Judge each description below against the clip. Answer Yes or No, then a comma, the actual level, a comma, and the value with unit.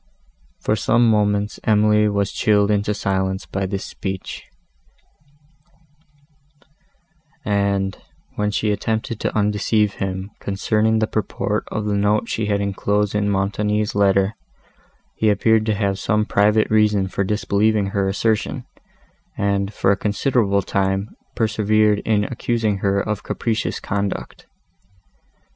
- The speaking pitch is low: Yes, low, 105 Hz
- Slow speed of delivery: Yes, slow, 125 wpm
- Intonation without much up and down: Yes, narrow, 1.4 semitones